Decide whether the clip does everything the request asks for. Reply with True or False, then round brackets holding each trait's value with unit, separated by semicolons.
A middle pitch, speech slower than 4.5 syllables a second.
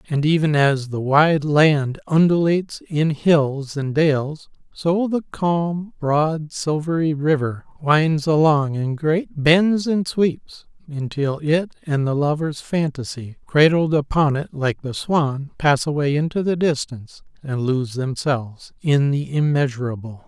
True (150 Hz; 3.8 syllables/s)